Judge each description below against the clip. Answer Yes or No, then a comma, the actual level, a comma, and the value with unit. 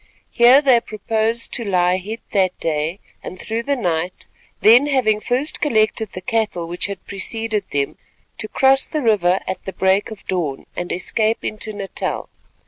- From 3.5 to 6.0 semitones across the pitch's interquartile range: Yes, average, 3.8 semitones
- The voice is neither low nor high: No, high, 215 Hz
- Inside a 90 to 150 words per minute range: No, average, 165 wpm